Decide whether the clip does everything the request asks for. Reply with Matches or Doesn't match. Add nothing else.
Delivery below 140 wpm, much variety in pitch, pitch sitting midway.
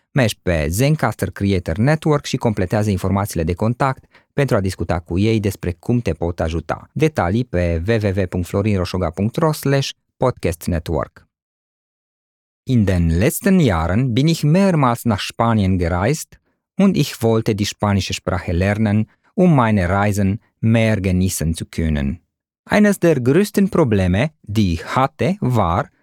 Doesn't match